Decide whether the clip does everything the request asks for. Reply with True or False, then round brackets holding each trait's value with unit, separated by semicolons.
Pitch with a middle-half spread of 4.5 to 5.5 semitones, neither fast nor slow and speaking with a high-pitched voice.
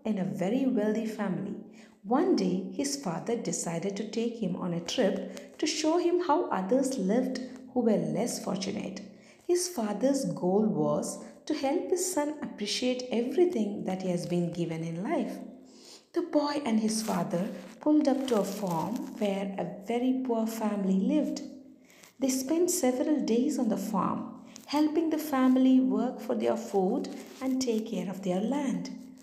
True (5.1 semitones; 160 wpm; 240 Hz)